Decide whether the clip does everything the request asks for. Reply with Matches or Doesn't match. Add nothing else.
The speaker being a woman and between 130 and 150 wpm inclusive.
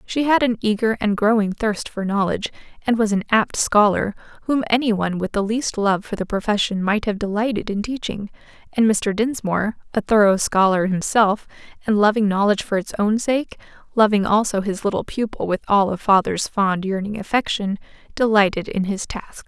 Doesn't match